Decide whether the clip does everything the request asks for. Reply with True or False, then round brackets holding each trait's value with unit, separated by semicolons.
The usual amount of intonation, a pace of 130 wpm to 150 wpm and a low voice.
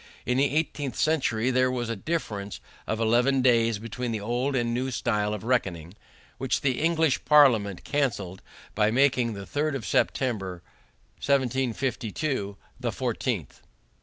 True (3.9 semitones; 145 wpm; 125 Hz)